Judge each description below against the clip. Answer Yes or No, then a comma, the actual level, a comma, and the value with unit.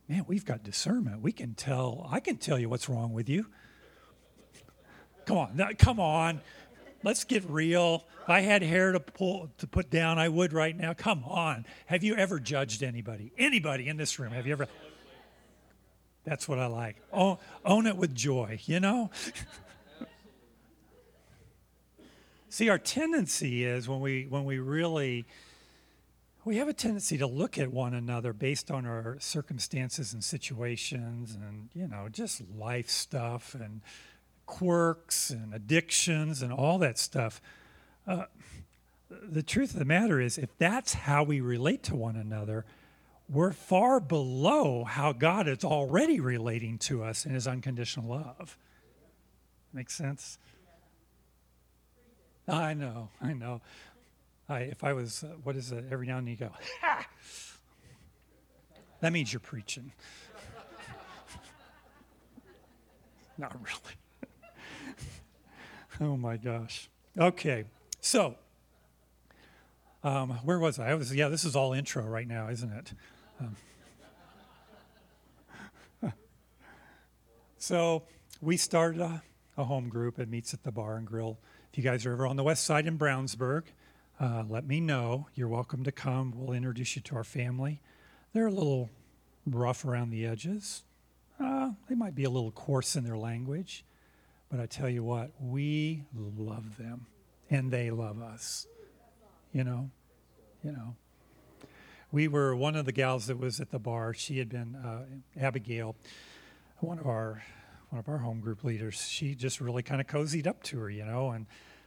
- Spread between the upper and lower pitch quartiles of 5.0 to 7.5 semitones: Yes, average, 5.3 semitones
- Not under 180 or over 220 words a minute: No, average, 150 wpm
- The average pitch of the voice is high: No, low, 130 Hz